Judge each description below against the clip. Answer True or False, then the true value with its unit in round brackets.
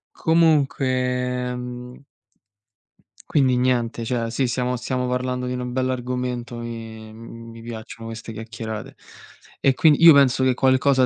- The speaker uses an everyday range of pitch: False (1.8 semitones)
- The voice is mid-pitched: False (125 Hz)